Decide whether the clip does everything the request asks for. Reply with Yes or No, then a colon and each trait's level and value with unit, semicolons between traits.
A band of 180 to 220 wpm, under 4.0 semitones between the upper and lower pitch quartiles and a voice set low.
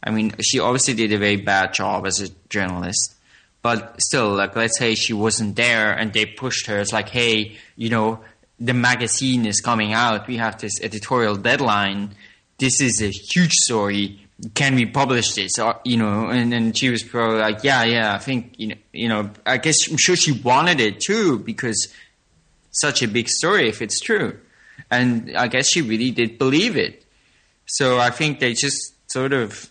Yes: average, 190 wpm; average, 2.9 semitones; low, 115 Hz